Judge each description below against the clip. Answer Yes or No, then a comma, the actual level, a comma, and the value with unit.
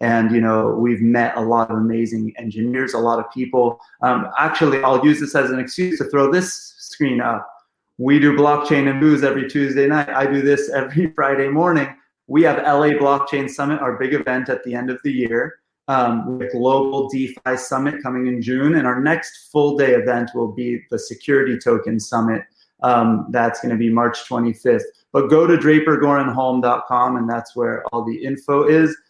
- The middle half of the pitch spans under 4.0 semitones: Yes, average, 3.3 semitones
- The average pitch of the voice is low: Yes, low, 130 Hz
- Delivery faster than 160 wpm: Yes, average, 190 wpm